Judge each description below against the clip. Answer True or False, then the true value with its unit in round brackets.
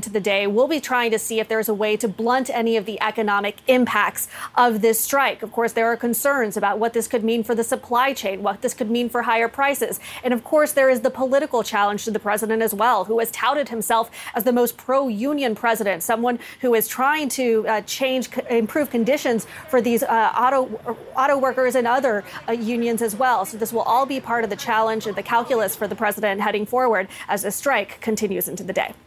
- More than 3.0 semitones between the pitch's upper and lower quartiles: False (2.7 semitones)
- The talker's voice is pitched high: True (230 Hz)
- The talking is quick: True (230 wpm)